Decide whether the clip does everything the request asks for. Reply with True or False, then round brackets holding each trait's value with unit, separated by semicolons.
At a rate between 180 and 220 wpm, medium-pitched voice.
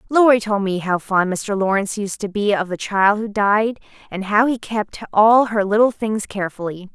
False (205 wpm; 205 Hz)